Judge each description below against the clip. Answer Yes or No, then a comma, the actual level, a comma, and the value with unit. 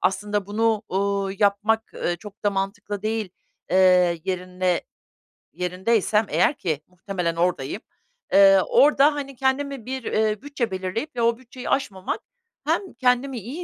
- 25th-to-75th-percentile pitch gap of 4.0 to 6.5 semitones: Yes, average, 4.3 semitones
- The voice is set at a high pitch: Yes, high, 205 Hz